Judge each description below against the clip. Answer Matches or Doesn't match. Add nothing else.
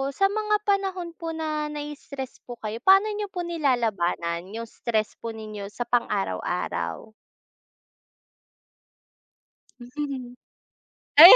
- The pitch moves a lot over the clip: Matches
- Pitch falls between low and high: Doesn't match